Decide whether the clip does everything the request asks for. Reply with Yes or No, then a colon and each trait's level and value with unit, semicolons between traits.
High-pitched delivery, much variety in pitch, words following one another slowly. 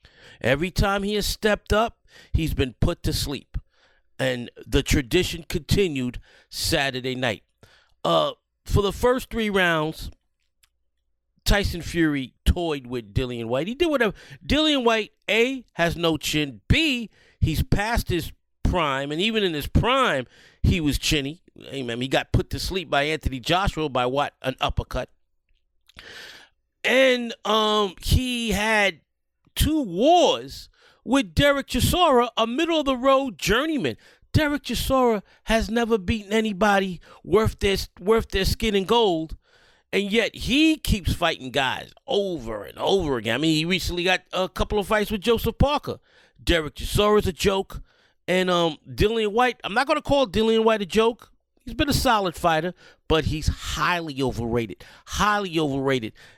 No: high, 195 Hz; wide, 7.1 semitones; average, 155 wpm